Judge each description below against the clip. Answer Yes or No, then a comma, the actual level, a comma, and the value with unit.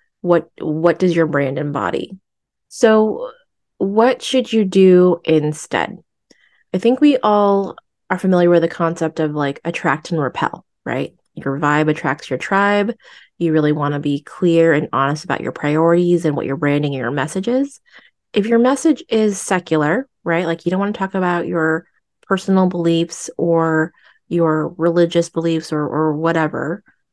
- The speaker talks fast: No, average, 165 wpm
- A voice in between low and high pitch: Yes, medium, 170 Hz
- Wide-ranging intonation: No, average, 3.8 semitones